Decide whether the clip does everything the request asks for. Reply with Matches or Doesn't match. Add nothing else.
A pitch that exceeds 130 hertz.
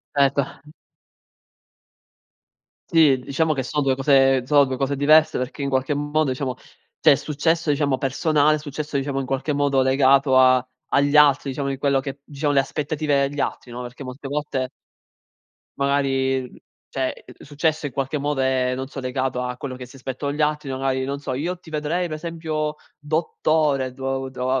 Matches